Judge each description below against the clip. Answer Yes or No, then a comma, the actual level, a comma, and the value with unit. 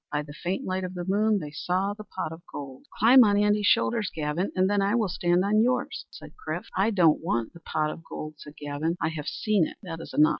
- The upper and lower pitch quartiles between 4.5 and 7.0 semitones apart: Yes, average, 4.9 semitones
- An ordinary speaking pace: No, fast, 250 wpm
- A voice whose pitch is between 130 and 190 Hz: Yes, medium, 185 Hz